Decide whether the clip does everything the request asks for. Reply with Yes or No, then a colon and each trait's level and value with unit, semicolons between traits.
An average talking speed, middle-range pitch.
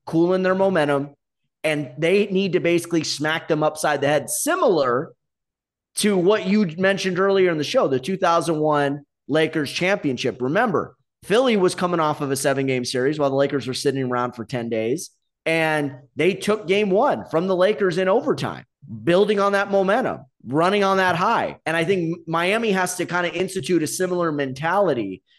Yes: average, 175 wpm; medium, 170 Hz